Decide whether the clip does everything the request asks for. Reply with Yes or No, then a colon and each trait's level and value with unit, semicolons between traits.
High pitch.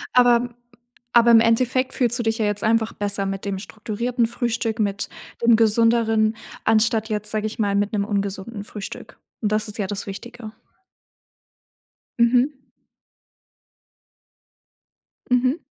Yes: high, 220 Hz